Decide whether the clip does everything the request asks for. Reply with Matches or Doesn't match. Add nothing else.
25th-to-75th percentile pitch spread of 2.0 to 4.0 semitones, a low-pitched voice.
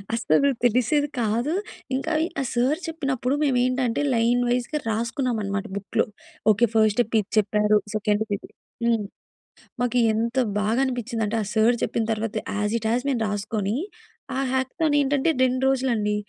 Doesn't match